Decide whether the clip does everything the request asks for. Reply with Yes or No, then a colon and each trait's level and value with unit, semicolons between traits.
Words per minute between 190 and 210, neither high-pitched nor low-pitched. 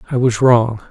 No: average, 200 wpm; low, 120 Hz